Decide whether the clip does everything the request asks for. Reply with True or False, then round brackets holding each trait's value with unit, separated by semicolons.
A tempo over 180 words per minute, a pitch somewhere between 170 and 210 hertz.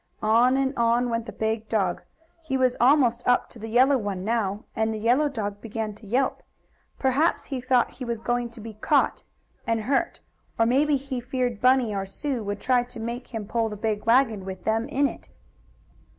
False (200 wpm; 235 Hz)